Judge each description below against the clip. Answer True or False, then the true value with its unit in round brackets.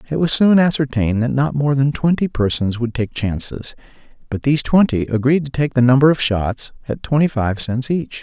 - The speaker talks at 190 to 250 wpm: True (205 wpm)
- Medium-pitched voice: False (130 Hz)